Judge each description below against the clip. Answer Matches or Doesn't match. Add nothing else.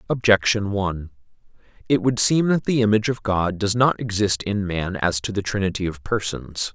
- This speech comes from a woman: Doesn't match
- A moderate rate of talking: Matches